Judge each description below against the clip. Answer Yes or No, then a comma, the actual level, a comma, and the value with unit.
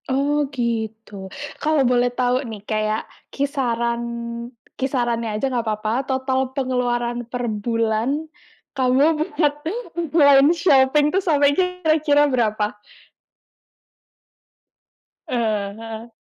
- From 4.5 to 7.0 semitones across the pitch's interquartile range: No, average, 4.0 semitones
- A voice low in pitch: No, very high, 250 Hz